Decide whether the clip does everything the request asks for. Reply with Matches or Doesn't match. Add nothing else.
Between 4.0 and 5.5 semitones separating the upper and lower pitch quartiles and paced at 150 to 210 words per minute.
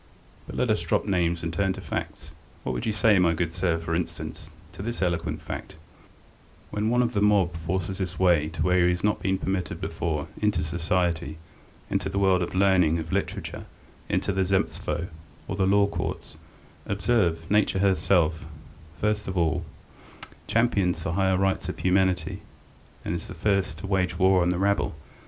Doesn't match